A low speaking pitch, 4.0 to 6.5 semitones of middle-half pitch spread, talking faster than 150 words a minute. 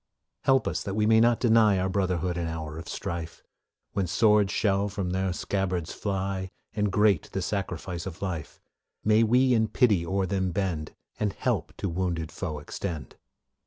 No: very low, 95 Hz; average, 3.1 semitones; average, 170 wpm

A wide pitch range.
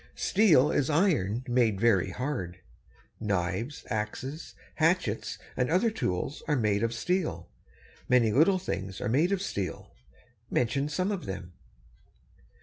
Yes: wide, 7.7 semitones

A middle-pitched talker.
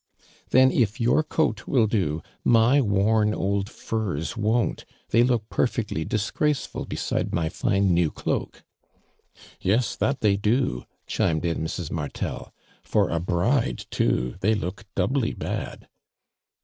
No: low, 105 Hz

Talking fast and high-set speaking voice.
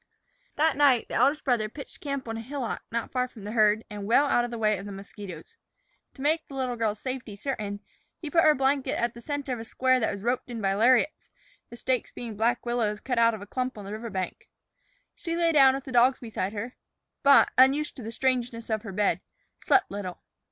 Yes: fast, 225 wpm; high, 240 Hz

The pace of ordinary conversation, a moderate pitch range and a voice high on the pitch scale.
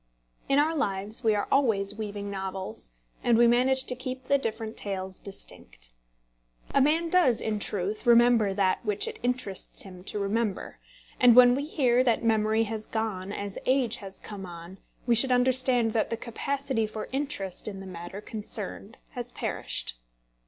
Yes: average, 165 wpm; average, 4.1 semitones; high, 220 Hz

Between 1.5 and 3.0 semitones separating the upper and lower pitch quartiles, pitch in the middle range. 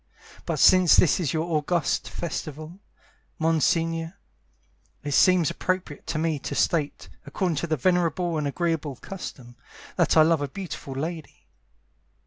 Yes: average, 2.7 semitones; medium, 165 Hz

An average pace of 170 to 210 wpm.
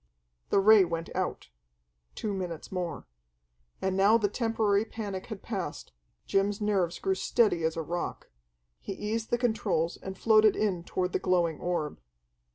No: average, 155 wpm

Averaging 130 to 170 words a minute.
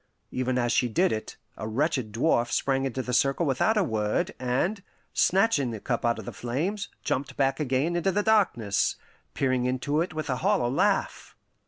No: average, 185 wpm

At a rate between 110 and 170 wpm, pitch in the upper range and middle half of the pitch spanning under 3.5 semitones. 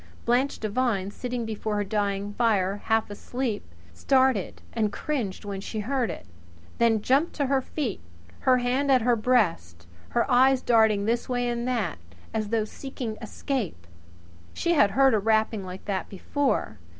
No: average, 160 wpm; high, 225 Hz; average, 3.8 semitones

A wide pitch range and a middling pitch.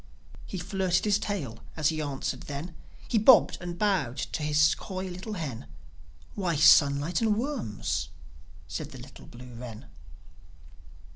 Yes: wide, 6.2 semitones; medium, 160 Hz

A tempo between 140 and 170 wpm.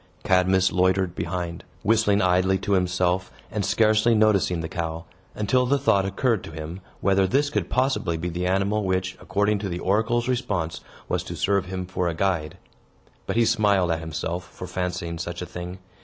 No: average, 180 wpm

